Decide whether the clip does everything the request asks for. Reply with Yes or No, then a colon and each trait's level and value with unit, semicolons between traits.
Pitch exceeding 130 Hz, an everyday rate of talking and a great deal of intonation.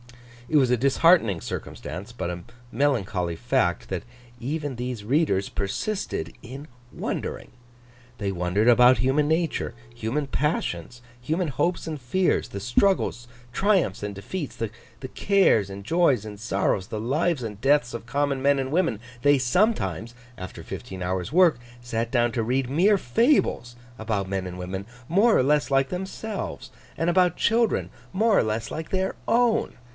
No: low, 125 Hz; average, 155 wpm; wide, 7.3 semitones